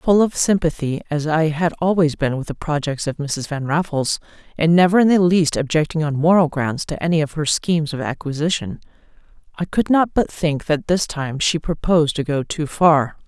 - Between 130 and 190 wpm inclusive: No, fast, 205 wpm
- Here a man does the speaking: No, female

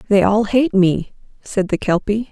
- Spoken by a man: No, female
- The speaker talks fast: No, average, 180 wpm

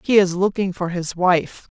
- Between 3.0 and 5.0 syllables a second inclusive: Yes, 4.4 syllables/s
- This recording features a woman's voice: Yes, female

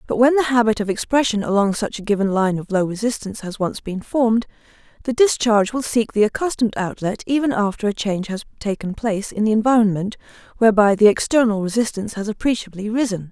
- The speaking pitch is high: Yes, high, 220 Hz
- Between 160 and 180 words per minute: No, average, 190 wpm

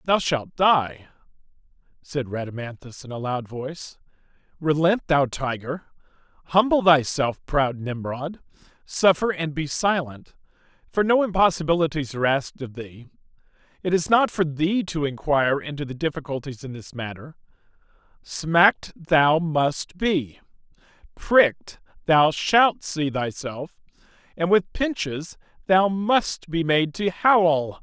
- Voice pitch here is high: No, medium, 155 Hz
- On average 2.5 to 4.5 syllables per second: Yes, 4.2 syllables/s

